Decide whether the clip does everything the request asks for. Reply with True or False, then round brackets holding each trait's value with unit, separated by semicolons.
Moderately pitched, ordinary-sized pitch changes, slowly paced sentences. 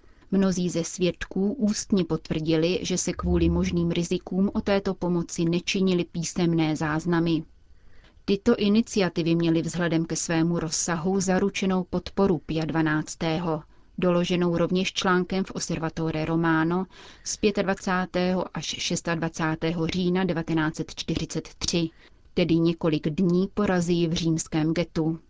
False (170 Hz; 2.3 semitones; 110 wpm)